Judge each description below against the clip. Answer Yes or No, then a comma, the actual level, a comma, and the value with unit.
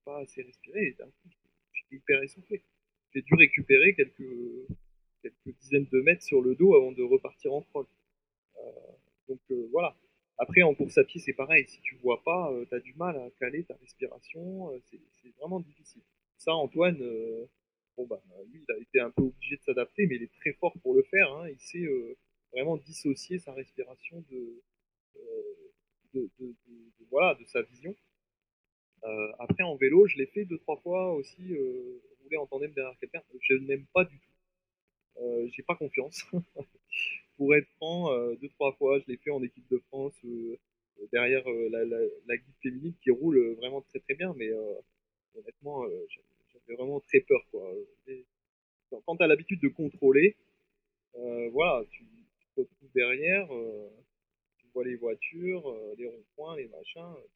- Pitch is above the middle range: No, medium, 175 Hz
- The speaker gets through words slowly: No, average, 190 wpm